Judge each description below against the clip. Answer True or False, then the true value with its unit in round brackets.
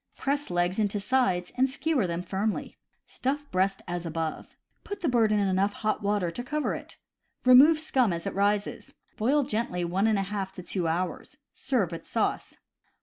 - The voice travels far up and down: True (5.8 semitones)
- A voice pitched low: False (205 Hz)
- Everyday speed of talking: True (180 wpm)